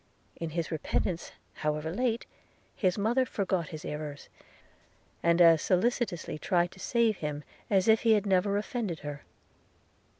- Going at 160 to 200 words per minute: No, average, 140 wpm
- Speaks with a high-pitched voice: No, medium, 180 Hz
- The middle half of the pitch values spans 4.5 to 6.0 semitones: Yes, average, 5.1 semitones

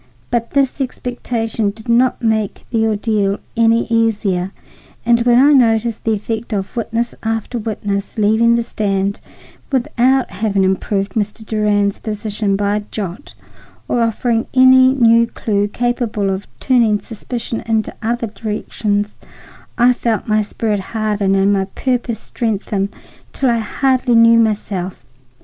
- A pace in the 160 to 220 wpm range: No, slow, 135 wpm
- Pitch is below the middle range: No, high, 220 Hz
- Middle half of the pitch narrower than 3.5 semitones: Yes, narrow, 2.4 semitones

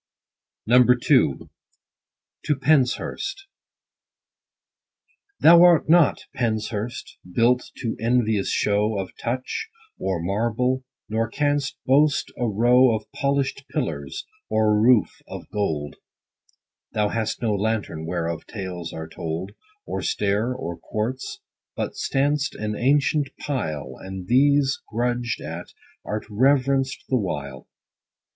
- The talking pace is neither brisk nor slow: No, slow, 115 wpm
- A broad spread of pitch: No, average, 4.9 semitones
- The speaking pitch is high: No, low, 115 Hz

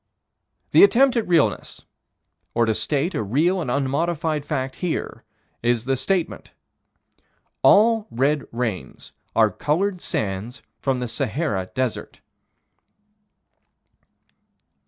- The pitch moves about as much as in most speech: No, wide, 6.4 semitones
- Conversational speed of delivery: No, slow, 110 wpm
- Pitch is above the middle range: No, medium, 140 Hz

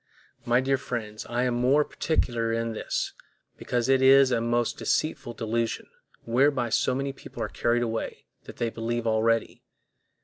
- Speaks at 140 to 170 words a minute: Yes, average, 160 wpm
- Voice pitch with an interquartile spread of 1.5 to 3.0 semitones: Yes, narrow, 2.4 semitones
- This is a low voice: Yes, low, 120 Hz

